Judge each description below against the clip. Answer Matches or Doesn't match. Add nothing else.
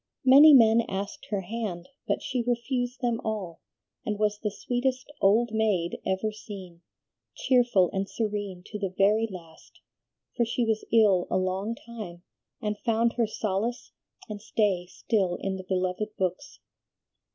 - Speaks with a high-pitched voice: Matches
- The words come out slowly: Doesn't match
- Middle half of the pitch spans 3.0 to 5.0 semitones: Matches